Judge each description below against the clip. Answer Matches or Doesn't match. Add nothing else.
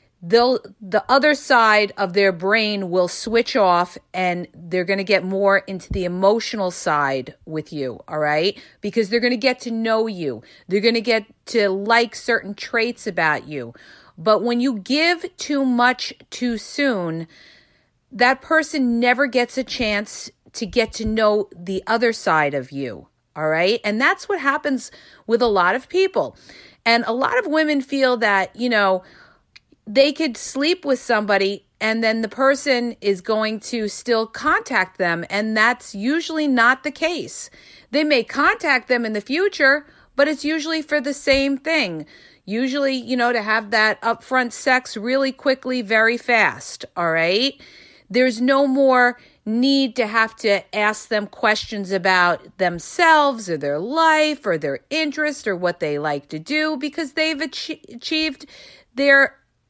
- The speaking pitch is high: Matches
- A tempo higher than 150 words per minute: Matches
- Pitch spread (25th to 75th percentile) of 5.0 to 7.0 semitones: Matches